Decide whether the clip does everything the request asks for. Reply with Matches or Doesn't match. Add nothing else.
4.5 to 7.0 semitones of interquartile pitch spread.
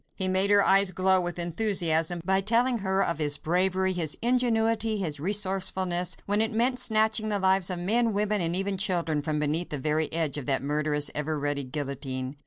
Matches